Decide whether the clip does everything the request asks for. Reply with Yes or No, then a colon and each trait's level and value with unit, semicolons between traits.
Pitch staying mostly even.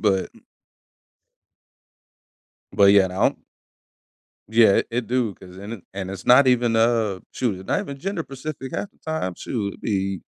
No: average, 4.6 semitones